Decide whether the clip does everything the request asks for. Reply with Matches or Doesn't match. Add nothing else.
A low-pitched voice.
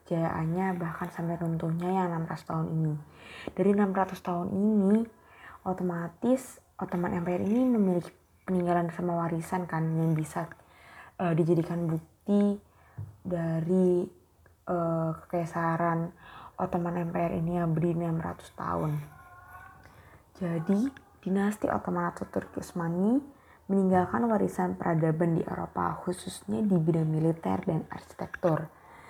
Doesn't match